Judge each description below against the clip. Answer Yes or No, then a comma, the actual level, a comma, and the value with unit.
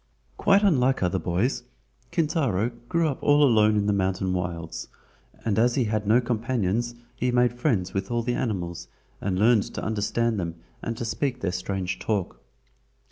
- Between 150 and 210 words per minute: Yes, average, 170 wpm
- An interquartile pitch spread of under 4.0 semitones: No, average, 4.3 semitones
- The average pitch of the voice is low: Yes, low, 110 Hz